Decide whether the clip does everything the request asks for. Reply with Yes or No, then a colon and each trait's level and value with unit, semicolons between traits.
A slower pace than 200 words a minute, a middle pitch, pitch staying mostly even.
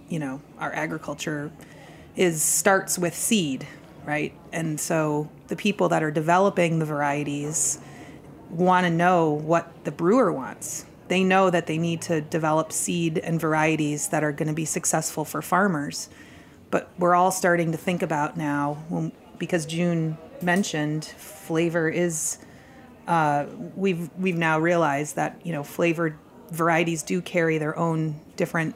Yes: average, 150 wpm; medium, 165 Hz; narrow, 2.3 semitones